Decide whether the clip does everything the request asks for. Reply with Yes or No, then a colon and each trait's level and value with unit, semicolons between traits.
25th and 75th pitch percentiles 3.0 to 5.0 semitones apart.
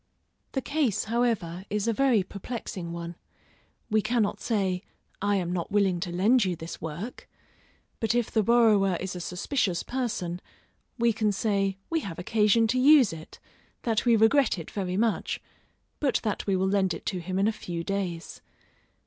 Yes: average, 4.2 semitones